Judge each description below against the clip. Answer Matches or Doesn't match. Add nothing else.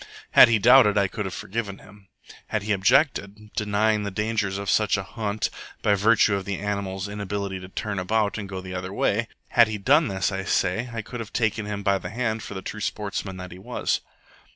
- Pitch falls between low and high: Doesn't match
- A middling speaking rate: Doesn't match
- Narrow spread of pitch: Matches